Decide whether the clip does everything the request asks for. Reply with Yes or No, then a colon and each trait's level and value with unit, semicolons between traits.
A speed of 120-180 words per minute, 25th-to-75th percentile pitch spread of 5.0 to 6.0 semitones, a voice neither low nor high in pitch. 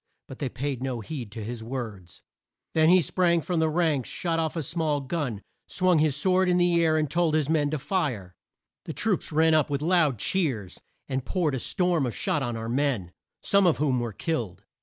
No: fast, 205 wpm; average, 5.3 semitones; medium, 150 Hz